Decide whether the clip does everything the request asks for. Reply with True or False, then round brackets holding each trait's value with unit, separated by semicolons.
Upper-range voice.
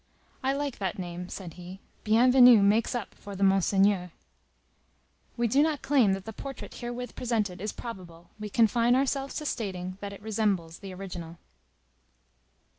True (205 Hz)